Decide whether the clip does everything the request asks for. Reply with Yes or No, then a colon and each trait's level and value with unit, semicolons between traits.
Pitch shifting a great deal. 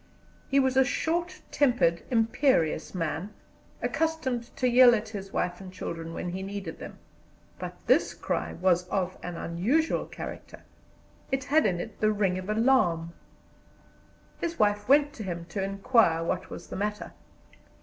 Yes: wide, 6.4 semitones